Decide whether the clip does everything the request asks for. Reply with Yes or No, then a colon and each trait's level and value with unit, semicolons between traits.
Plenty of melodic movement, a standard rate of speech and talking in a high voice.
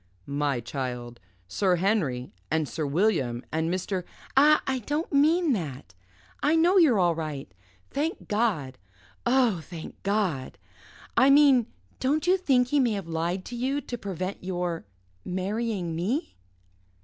Yes: wide, 8.5 semitones; average, 145 wpm; high, 195 Hz